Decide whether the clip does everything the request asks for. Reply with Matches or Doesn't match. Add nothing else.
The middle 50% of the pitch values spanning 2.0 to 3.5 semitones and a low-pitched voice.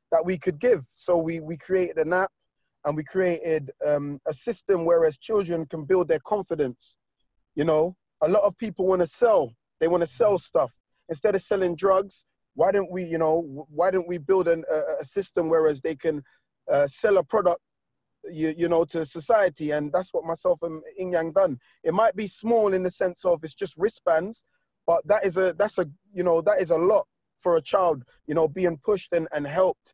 Doesn't match